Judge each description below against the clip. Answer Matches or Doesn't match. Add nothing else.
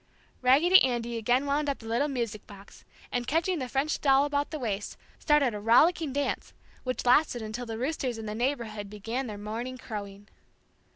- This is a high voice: Matches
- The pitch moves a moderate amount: Matches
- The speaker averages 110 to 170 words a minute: Doesn't match